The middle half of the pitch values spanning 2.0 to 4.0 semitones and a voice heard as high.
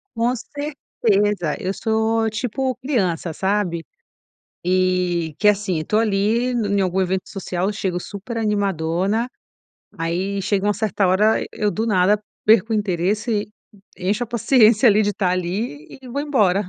Yes: average, 3.3 semitones; high, 205 Hz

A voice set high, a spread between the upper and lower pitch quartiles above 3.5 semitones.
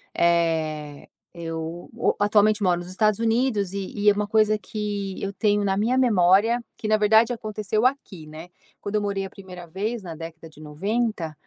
Yes: high, 200 Hz; average, 3.9 semitones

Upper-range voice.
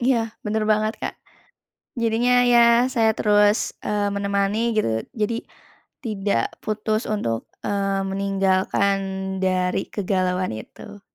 Yes: high, 205 Hz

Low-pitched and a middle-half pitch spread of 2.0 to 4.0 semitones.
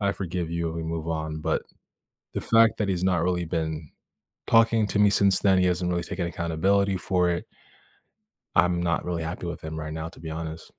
Yes: very low, 85 Hz; narrow, 2.6 semitones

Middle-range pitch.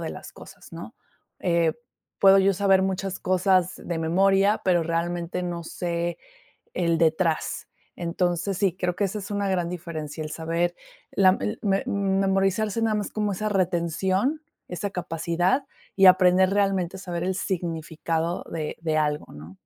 Yes: medium, 180 Hz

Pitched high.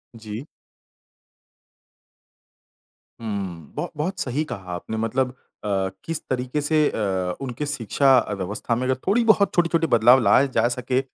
No: low, 125 Hz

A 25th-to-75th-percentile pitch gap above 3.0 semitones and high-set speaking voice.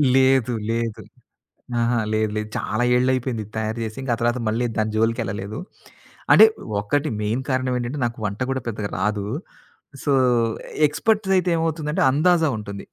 No: average, 3.7 semitones; low, 120 Hz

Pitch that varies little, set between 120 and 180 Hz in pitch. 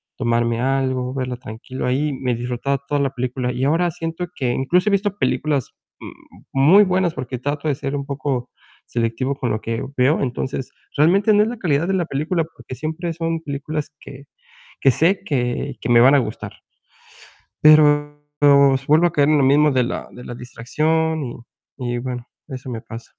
No: average, 3.7 semitones; medium, 140 Hz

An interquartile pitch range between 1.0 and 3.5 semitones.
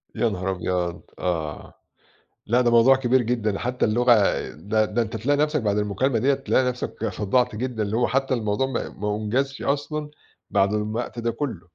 No: average, 3.9 semitones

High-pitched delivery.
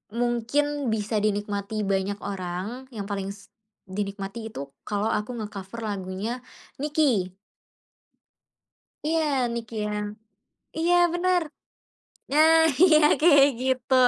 Yes: high, 220 Hz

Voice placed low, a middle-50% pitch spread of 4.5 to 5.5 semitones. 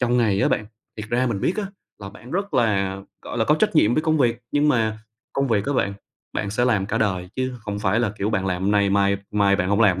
No: low, 105 Hz; average, 3.7 semitones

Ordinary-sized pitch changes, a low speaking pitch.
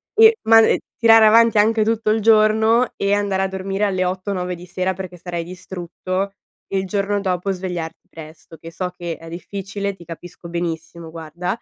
No: average, 3.1 semitones; high, 190 Hz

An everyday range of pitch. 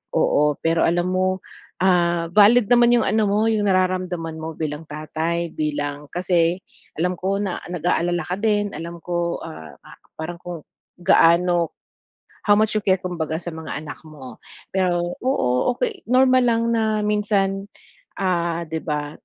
Yes: average, 3.4 semitones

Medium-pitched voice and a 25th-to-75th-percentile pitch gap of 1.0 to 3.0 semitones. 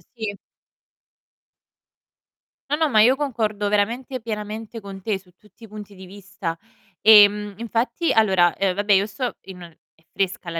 No: high, 210 Hz; narrow, 2.6 semitones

